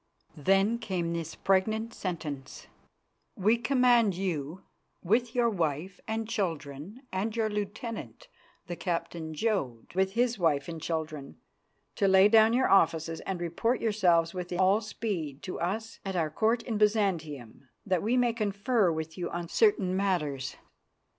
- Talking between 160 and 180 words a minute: No, average, 145 wpm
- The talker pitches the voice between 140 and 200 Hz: Yes, high, 190 Hz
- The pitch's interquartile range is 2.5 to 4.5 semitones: No, average, 5.0 semitones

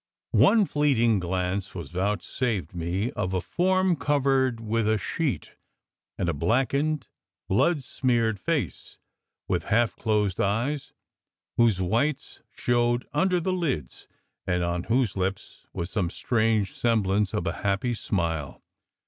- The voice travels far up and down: Yes, wide, 6.1 semitones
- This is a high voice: No, low, 110 Hz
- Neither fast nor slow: No, slow, 130 wpm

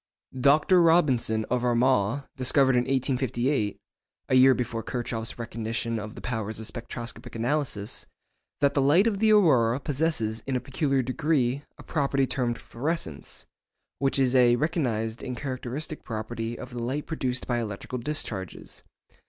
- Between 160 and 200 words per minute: No, average, 145 wpm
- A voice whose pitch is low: Yes, low, 125 Hz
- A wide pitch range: No, average, 3.4 semitones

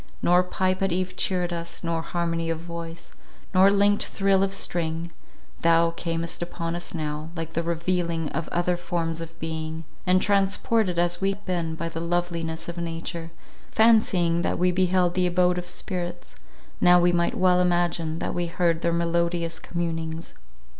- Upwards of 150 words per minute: Yes, average, 165 wpm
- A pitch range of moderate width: No, narrow, 1.4 semitones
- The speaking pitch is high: No, medium, 170 Hz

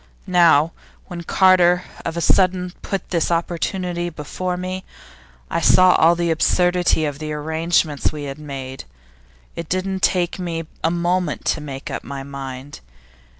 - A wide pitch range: No, average, 3.1 semitones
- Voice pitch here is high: No, medium, 170 Hz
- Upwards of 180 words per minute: No, average, 150 wpm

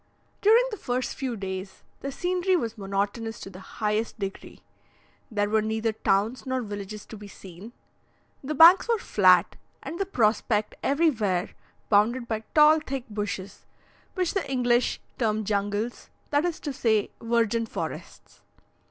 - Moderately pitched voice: No, high, 225 Hz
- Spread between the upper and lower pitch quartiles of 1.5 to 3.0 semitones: No, average, 4.9 semitones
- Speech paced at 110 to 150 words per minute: Yes, average, 145 wpm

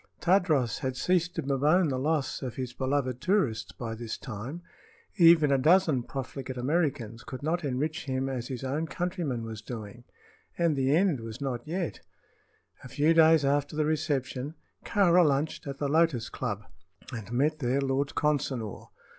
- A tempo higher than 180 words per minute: No, average, 165 wpm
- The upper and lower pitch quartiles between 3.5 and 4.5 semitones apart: Yes, average, 4.0 semitones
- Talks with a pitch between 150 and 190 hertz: No, medium, 140 Hz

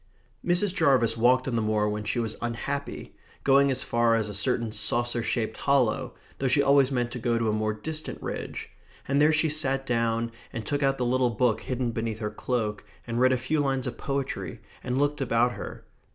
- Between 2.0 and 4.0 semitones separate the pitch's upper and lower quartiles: Yes, average, 3.0 semitones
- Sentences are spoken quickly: Yes, fast, 210 wpm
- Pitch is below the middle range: Yes, low, 125 Hz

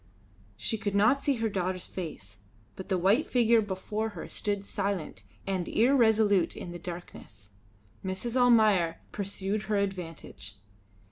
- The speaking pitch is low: No, high, 200 Hz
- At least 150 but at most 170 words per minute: No, slow, 135 wpm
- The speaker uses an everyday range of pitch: Yes, average, 3.5 semitones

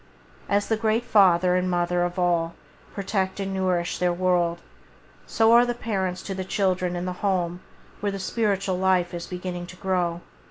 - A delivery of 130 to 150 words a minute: No, average, 175 wpm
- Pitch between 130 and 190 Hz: Yes, medium, 185 Hz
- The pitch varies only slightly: Yes, narrow, 1.8 semitones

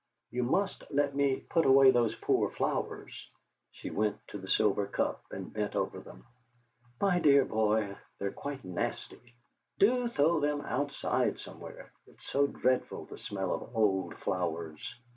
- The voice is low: Yes, low, 125 Hz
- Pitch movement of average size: No, wide, 5.9 semitones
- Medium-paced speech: Yes, average, 150 wpm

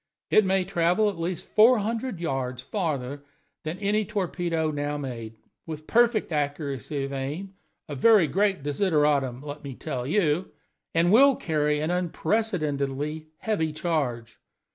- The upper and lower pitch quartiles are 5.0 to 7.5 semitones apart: Yes, average, 5.3 semitones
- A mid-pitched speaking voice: Yes, medium, 155 Hz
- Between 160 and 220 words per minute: No, average, 140 wpm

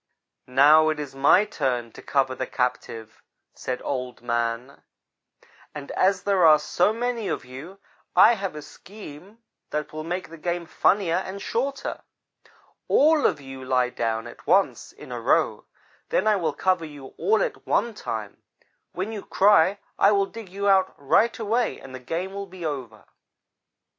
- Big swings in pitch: Yes, wide, 7.1 semitones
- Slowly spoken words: No, average, 170 wpm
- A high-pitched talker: No, medium, 165 Hz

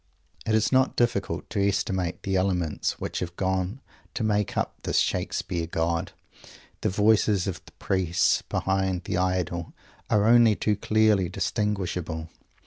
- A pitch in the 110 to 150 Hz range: No, very low, 95 Hz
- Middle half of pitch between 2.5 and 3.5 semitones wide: Yes, average, 3.0 semitones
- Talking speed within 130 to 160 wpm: Yes, average, 140 wpm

